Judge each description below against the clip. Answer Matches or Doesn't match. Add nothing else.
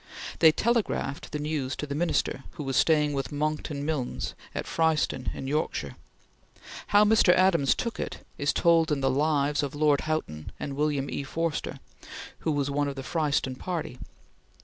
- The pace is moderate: Matches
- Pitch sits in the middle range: Matches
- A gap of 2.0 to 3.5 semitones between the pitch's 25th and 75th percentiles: Matches